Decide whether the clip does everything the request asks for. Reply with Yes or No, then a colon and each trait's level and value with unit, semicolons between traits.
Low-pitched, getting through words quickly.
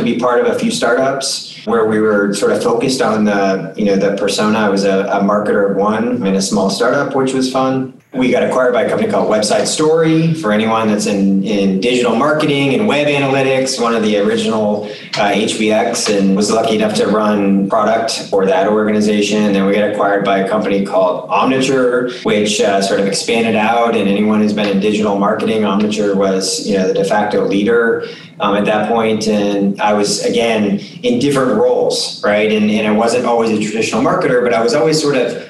Yes: low, 110 Hz; fast, 215 wpm